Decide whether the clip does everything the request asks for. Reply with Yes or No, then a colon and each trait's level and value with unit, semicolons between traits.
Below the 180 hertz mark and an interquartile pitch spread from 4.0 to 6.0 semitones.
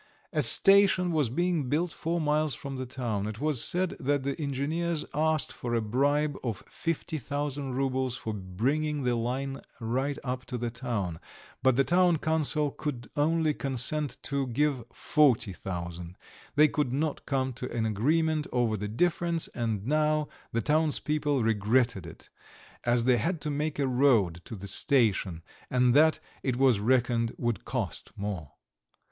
Yes: low, 135 Hz; average, 4.6 semitones